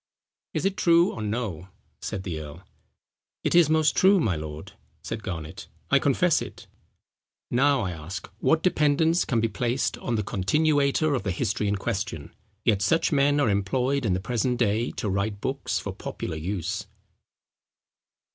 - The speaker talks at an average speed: Yes, average, 165 wpm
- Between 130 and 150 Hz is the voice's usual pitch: No, low, 110 Hz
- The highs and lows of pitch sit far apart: Yes, wide, 6.9 semitones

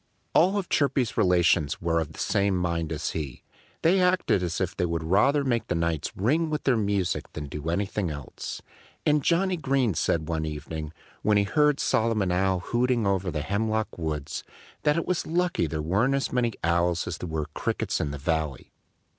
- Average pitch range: No, wide, 7.8 semitones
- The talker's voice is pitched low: Yes, very low, 95 Hz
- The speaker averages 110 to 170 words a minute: No, average, 190 wpm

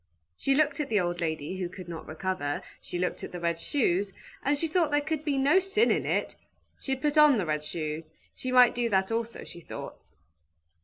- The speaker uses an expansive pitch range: Yes, wide, 8.9 semitones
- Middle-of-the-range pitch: No, high, 220 Hz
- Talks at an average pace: No, fast, 215 wpm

